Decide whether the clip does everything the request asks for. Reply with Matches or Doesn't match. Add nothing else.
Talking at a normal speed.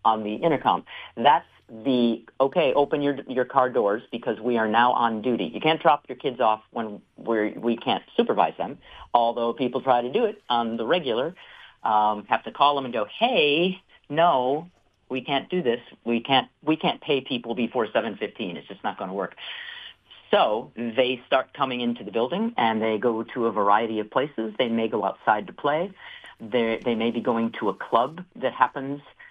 Matches